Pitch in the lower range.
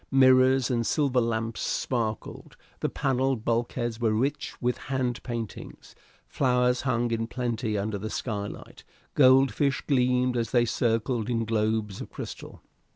Yes: low, 120 Hz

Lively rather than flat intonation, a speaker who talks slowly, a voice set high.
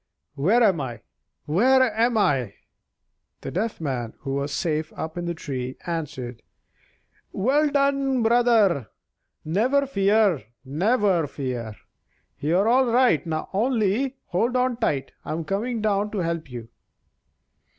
Yes: wide, 8.6 semitones; slow, 125 wpm; high, 195 Hz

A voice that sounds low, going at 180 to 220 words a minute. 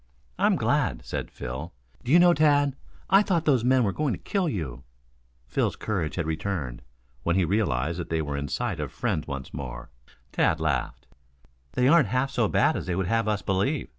Yes: very low, 95 Hz; average, 195 wpm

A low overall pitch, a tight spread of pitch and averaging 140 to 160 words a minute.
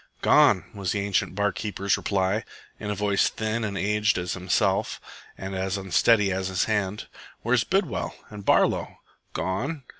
Yes: low, 100 Hz; narrow, 2.2 semitones; average, 155 wpm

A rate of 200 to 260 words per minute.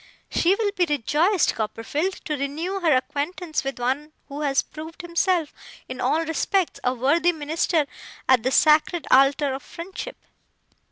No: average, 150 wpm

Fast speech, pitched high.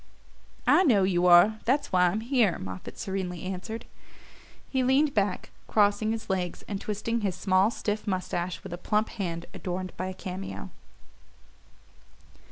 No: average, 150 wpm; high, 195 Hz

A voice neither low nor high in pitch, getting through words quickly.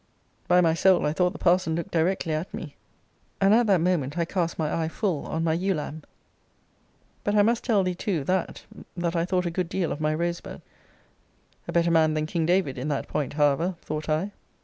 Yes: medium, 170 Hz; fast, 215 wpm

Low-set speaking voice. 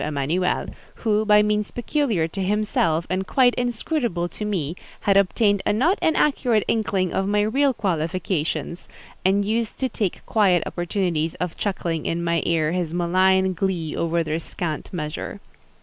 No: high, 190 Hz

